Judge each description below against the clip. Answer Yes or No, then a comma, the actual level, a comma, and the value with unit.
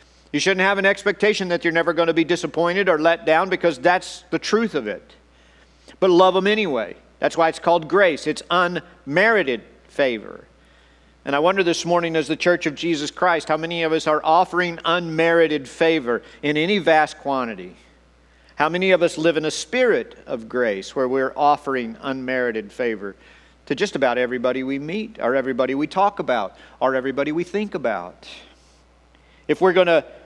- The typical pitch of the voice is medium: Yes, medium, 160 Hz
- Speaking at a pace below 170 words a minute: No, average, 180 wpm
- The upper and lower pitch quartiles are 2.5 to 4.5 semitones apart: No, wide, 5.5 semitones